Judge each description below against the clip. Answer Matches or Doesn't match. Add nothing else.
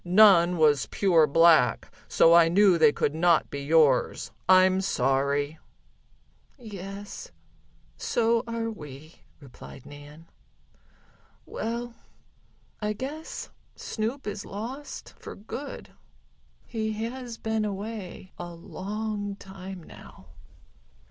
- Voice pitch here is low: Doesn't match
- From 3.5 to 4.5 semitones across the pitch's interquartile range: Doesn't match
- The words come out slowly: Matches